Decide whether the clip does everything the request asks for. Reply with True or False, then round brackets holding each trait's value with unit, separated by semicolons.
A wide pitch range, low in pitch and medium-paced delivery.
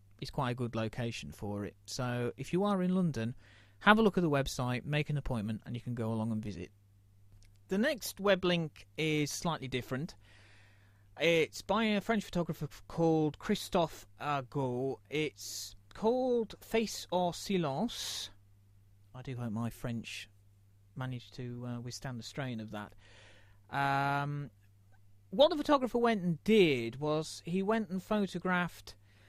True (8.8 semitones; 125 Hz; 150 wpm)